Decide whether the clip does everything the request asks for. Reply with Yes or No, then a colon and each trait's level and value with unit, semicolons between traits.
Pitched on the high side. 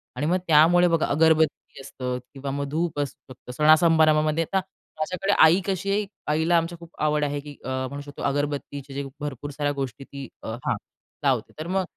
No: medium, 150 Hz